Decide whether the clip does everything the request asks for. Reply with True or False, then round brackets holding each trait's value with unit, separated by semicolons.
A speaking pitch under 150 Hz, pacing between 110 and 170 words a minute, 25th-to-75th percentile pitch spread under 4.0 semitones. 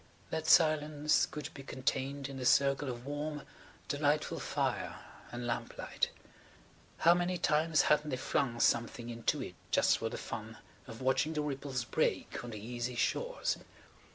True (140 Hz; 155 wpm; 3.6 semitones)